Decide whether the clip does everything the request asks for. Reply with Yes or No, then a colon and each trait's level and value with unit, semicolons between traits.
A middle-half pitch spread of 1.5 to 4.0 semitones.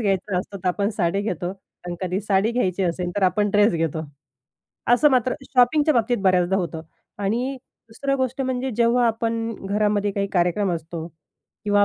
No: average, 4.4 semitones